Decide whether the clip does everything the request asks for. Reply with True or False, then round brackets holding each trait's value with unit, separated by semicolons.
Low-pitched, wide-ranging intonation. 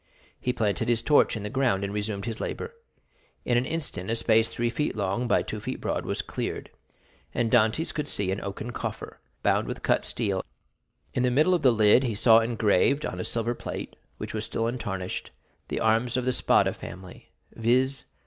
False (115 Hz; 3.2 semitones)